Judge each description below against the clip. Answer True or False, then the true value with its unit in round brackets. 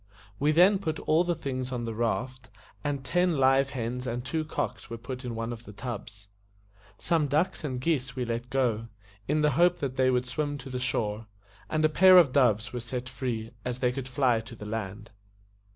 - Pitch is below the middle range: True (130 Hz)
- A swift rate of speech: True (210 wpm)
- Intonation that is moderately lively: True (3.8 semitones)